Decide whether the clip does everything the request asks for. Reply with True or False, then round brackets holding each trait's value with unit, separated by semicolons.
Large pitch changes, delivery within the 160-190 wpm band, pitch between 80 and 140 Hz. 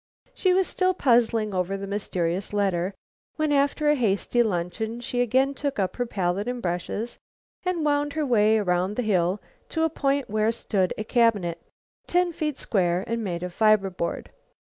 False (6.3 semitones; 175 wpm; 220 Hz)